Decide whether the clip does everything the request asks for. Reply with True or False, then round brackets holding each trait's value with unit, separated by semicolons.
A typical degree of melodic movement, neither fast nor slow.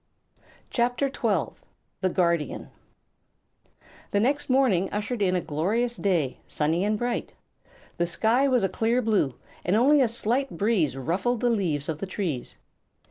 False (5.9 semitones; 145 wpm)